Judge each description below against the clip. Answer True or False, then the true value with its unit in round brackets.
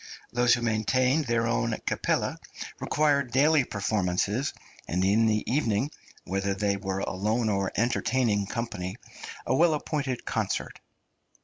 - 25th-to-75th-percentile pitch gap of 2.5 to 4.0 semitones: False (4.4 semitones)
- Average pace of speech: False (125 wpm)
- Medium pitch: False (115 Hz)